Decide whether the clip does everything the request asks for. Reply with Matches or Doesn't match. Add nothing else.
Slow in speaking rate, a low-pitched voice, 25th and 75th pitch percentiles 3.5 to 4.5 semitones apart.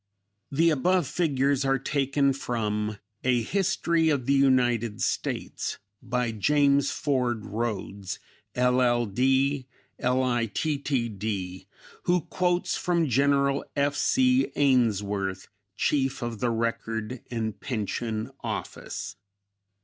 Matches